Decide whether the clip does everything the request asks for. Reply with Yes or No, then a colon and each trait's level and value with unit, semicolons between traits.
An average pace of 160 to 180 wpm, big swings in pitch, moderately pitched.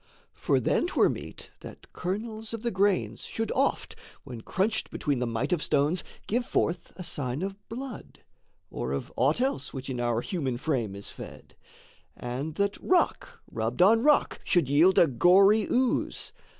Yes: average, 165 wpm; wide, 8.9 semitones; medium, 175 Hz